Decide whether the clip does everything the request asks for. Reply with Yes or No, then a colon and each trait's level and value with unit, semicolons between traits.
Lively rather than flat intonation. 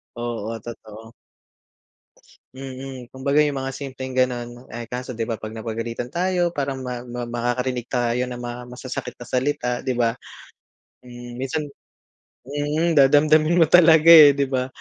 No: average, 2.8 semitones